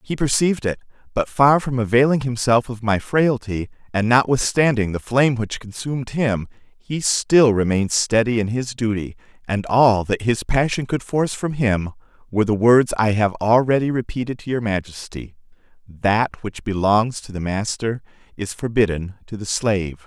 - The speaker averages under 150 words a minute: No, average, 165 wpm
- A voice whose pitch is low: Yes, low, 115 Hz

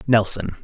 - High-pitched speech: No, low, 110 Hz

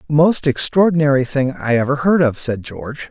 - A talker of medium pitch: Yes, medium, 145 Hz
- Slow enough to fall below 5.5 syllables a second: Yes, 5.2 syllables/s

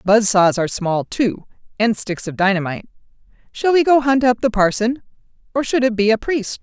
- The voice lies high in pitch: Yes, high, 220 Hz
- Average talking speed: Yes, average, 190 wpm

